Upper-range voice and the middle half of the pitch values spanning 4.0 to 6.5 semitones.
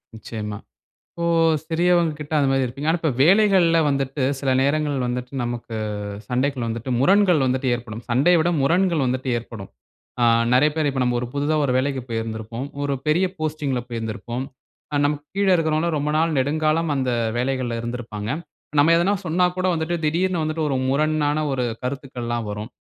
No: medium, 140 Hz; average, 4.4 semitones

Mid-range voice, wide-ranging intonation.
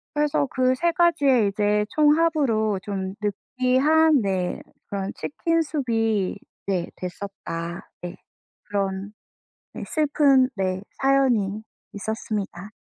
No: high, 220 Hz; wide, 6.2 semitones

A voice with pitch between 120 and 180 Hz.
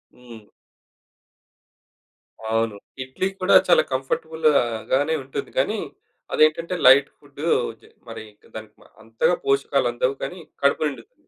Yes: low, 135 Hz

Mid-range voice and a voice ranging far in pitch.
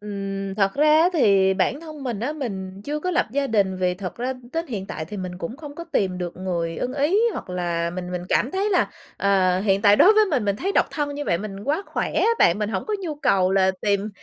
No: high, 205 Hz; wide, 7.6 semitones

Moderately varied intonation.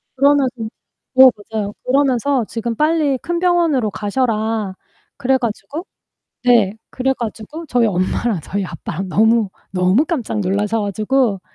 Yes: average, 4.7 semitones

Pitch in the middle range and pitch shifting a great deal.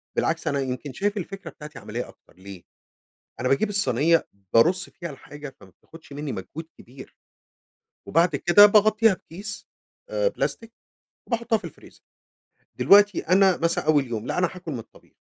Yes: medium, 170 Hz; wide, 6.9 semitones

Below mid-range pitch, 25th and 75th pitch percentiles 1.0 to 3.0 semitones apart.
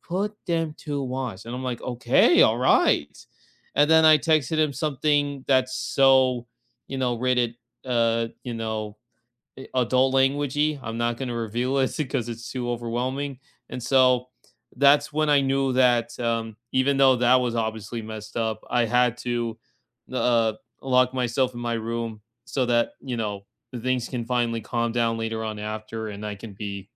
Yes: low, 120 Hz; average, 2.7 semitones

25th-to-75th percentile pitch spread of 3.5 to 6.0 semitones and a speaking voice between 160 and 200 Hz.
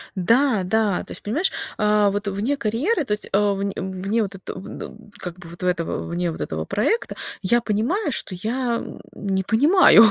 No: average, 3.9 semitones; high, 210 Hz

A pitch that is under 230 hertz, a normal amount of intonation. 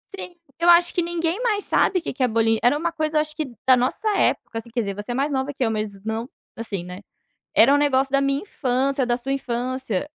No: very high, 265 Hz; average, 5.0 semitones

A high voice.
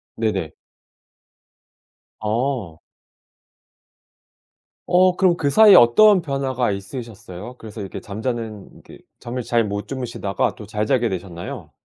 No: low, 115 Hz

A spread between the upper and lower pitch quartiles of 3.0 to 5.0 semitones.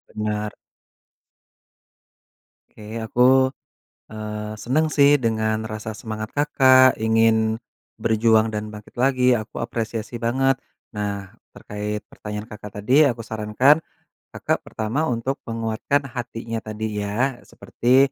No: narrow, 2.6 semitones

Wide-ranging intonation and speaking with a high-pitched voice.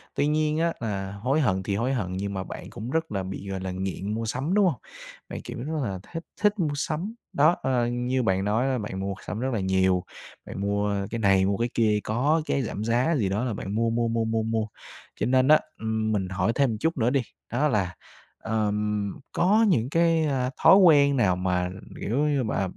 No: wide, 6.0 semitones; low, 115 Hz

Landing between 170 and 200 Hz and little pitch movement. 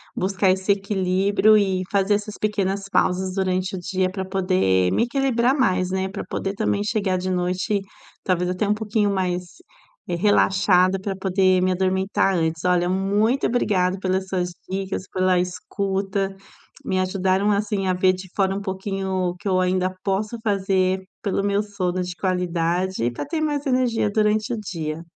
Yes: high, 190 Hz; narrow, 1.7 semitones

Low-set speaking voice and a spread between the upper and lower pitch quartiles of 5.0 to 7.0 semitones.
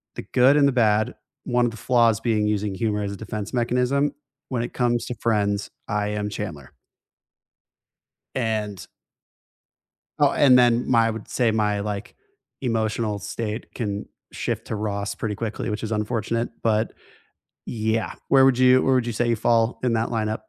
No: low, 115 Hz; narrow, 2.4 semitones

